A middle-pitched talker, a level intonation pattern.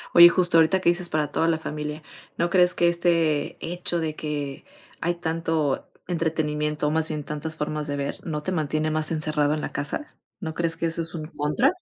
Yes: medium, 160 Hz; narrow, 2.2 semitones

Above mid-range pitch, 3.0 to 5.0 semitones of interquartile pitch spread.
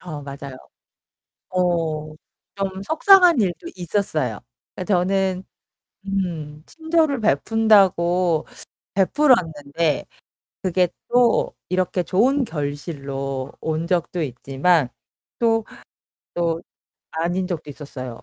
No: medium, 175 Hz; average, 4.6 semitones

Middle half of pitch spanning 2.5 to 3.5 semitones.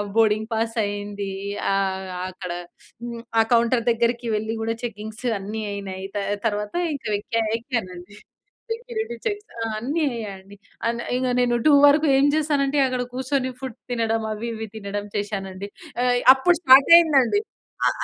No: average, 4.2 semitones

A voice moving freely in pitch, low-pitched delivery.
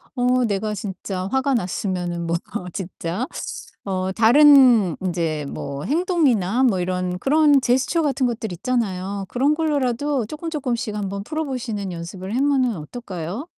No: wide, 6.3 semitones; high, 225 Hz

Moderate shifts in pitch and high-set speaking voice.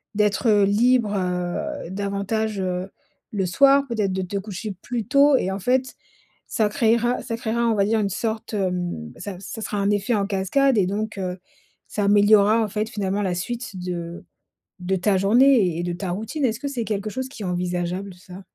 Yes: average, 3.4 semitones; high, 205 Hz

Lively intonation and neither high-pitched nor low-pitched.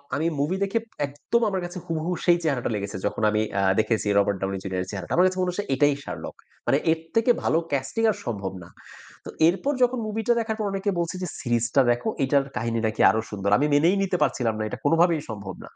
Yes: wide, 9.0 semitones; medium, 145 Hz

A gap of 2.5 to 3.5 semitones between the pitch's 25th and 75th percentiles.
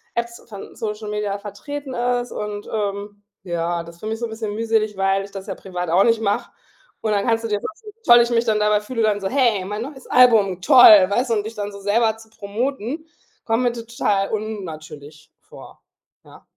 Yes: average, 2.8 semitones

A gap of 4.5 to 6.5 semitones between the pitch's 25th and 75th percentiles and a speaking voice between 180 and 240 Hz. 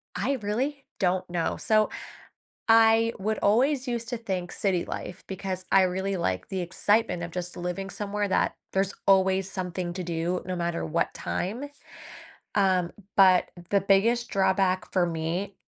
No: narrow, 2.6 semitones; high, 190 Hz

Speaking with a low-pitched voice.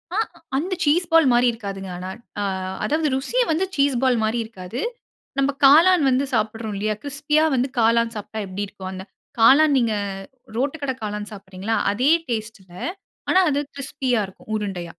No: high, 235 Hz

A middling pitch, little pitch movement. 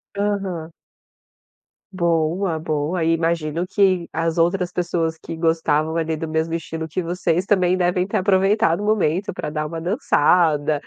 Yes: medium, 170 Hz; narrow, 2.3 semitones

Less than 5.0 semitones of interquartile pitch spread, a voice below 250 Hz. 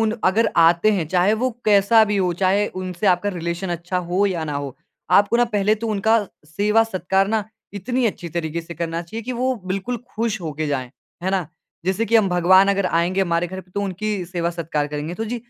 Yes: average, 3.6 semitones; high, 190 Hz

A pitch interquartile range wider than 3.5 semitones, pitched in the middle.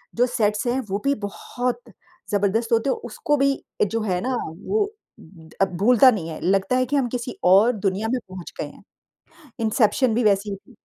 No: average, 4.1 semitones; high, 225 Hz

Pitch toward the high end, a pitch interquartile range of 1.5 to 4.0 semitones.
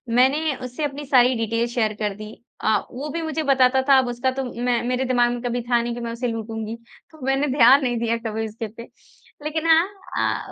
Yes: high, 245 Hz; average, 2.8 semitones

